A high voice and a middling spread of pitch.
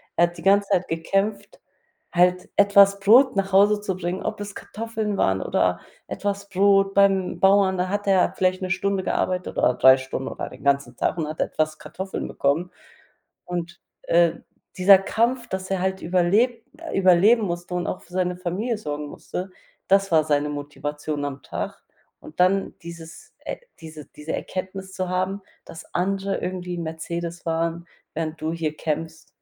No: medium, 180 Hz; average, 3.2 semitones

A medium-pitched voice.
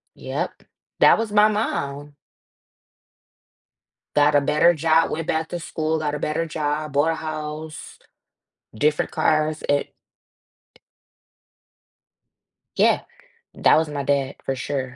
Yes: medium, 155 Hz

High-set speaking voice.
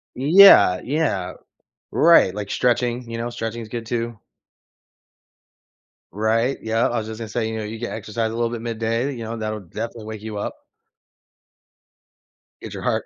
No: low, 115 Hz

